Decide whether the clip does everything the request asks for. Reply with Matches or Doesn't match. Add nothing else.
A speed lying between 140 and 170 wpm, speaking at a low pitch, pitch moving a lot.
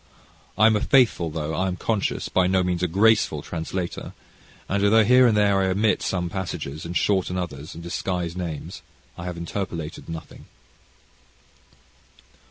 Doesn't match